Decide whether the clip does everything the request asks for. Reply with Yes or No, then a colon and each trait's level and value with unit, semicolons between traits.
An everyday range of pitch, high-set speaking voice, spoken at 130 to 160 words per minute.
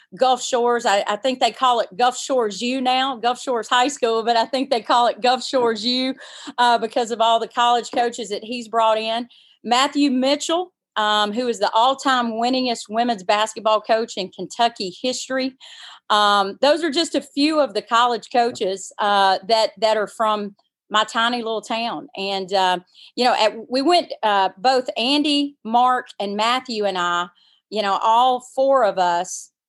No: average, 3.2 semitones; high, 235 Hz; average, 180 wpm